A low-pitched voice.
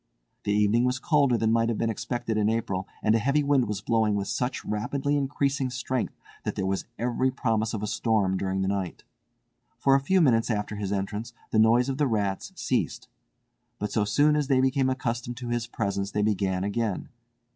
Yes: low, 115 Hz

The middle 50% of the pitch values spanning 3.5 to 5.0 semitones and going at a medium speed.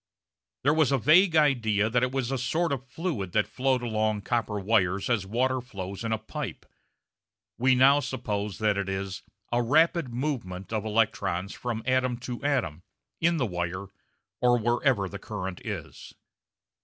Yes: average, 4.6 semitones; average, 165 wpm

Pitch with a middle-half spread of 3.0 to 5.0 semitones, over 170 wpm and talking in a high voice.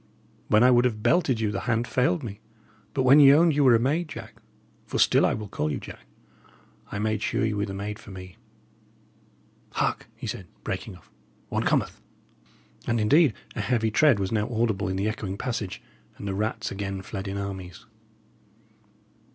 No: average, 4.1 semitones; average, 190 wpm; low, 110 Hz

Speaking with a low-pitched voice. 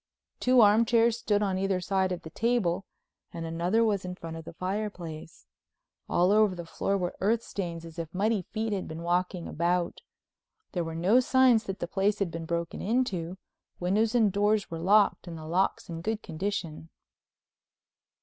No: high, 190 Hz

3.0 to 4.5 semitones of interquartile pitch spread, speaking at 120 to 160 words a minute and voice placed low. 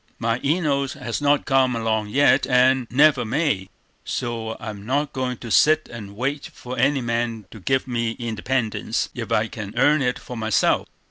No: average, 3.3 semitones; average, 175 wpm; low, 125 Hz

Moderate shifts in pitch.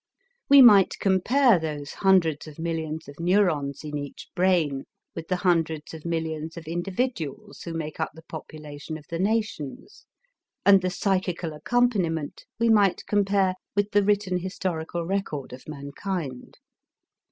Yes: average, 4.1 semitones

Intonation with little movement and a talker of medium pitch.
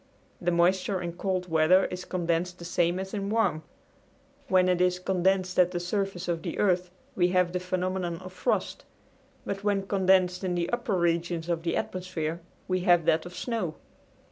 Yes: narrow, 1.5 semitones; medium, 180 Hz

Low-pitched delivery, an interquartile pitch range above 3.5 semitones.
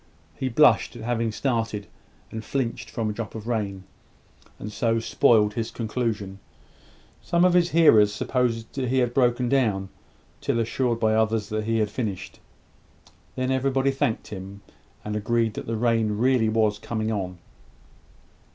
No: low, 115 Hz; average, 2.8 semitones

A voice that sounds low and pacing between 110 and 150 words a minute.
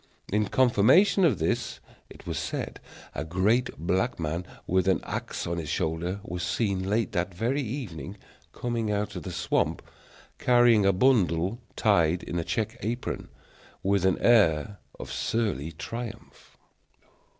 Yes: low, 100 Hz; average, 145 wpm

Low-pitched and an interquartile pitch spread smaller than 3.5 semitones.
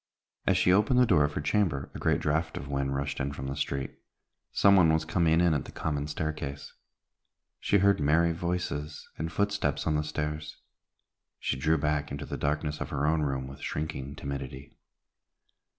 Yes: very low, 75 Hz; narrow, 2.6 semitones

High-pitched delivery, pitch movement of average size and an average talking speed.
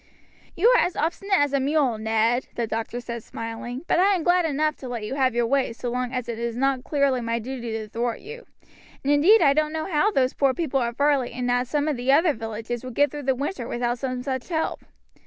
No: very high, 260 Hz; average, 3.8 semitones; fast, 245 wpm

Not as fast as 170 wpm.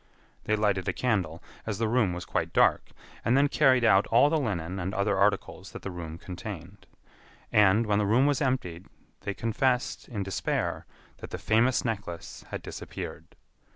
No: average, 175 wpm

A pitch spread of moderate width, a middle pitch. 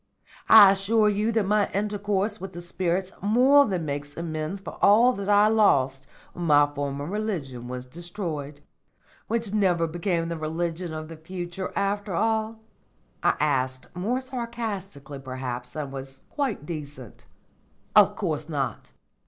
No: wide, 6.1 semitones; medium, 175 Hz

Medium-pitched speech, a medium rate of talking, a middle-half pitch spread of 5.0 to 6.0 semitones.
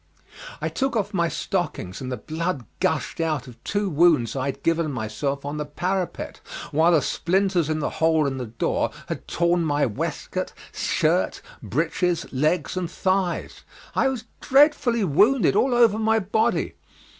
Yes: medium, 170 Hz; average, 160 wpm; wide, 5.4 semitones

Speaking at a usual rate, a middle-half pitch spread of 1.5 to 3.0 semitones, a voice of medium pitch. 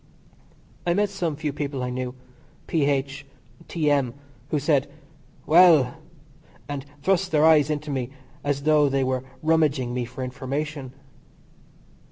No: slow, 130 wpm; average, 2.7 semitones; medium, 145 Hz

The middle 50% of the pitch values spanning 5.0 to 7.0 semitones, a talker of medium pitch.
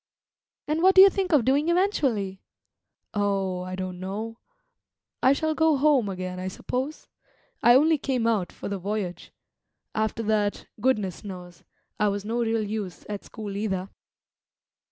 No: wide, 5.6 semitones; high, 215 Hz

